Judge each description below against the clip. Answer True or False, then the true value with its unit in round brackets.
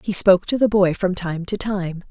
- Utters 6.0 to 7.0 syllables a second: False (5.1 syllables/s)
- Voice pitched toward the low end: False (190 Hz)